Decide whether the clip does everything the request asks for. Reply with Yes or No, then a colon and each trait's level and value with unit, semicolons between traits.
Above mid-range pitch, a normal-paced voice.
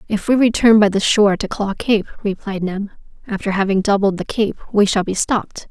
No: high, 205 Hz; fast, 210 wpm